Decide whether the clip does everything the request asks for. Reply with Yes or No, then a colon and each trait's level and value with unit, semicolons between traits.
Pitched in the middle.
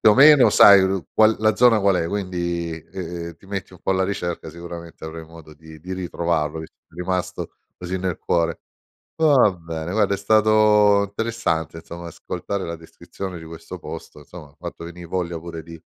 No: very low, 90 Hz